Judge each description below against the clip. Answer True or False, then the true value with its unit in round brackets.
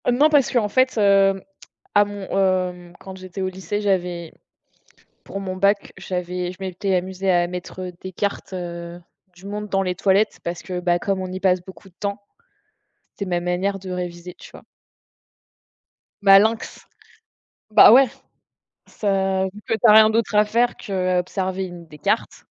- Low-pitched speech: False (190 Hz)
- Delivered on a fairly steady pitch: True (2.1 semitones)